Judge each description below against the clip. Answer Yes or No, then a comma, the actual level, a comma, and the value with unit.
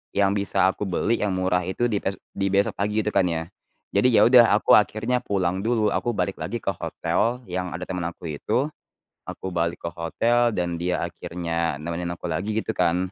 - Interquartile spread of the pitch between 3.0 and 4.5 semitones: Yes, average, 3.6 semitones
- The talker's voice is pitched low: Yes, very low, 95 Hz